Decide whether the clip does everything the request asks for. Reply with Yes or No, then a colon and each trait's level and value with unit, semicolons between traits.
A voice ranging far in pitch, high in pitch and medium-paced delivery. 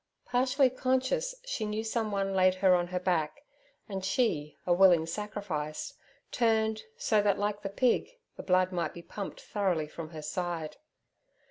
No: average, 4.1 semitones; high, 195 Hz; average, 155 wpm